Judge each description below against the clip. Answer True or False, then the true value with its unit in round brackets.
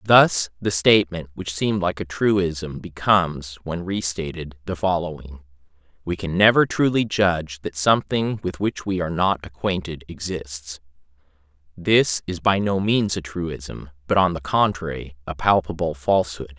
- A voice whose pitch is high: False (85 Hz)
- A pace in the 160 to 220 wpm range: False (150 wpm)